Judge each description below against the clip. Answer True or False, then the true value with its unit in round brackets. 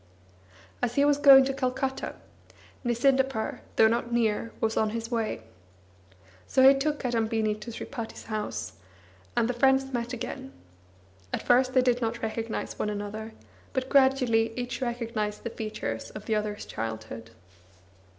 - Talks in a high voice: True (235 Hz)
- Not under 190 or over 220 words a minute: False (150 wpm)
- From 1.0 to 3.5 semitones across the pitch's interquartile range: True (3.1 semitones)